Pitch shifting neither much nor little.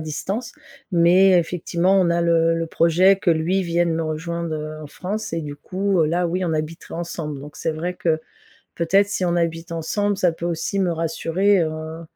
No: narrow, 2.2 semitones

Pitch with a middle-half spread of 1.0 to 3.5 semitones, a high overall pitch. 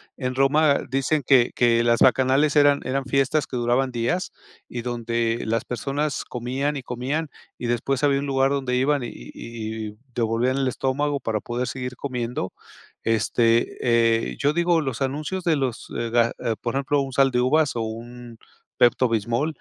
No: average, 2.9 semitones; low, 125 Hz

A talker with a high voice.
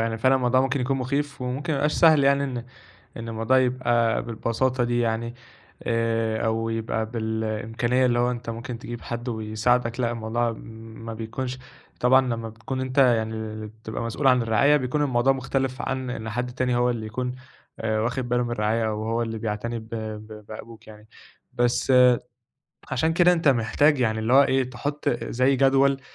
No: low, 120 Hz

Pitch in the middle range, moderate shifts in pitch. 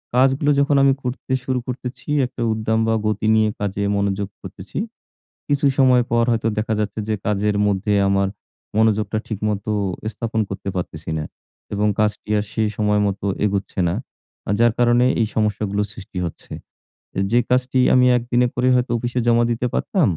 No: low, 110 Hz; average, 3.2 semitones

